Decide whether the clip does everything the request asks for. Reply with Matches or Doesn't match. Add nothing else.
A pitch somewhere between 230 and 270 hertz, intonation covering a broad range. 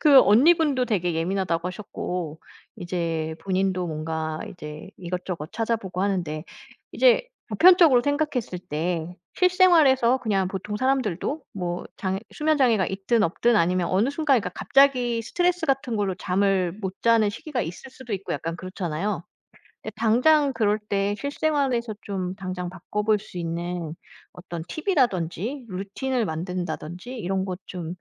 Doesn't match